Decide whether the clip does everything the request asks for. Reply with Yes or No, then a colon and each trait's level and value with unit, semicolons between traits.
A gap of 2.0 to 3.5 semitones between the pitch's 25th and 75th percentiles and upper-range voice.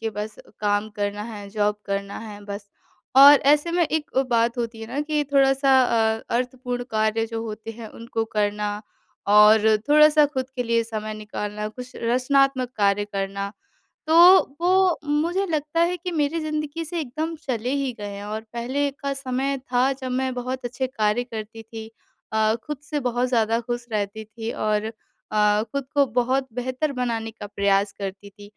No: average, 4.5 semitones; high, 235 Hz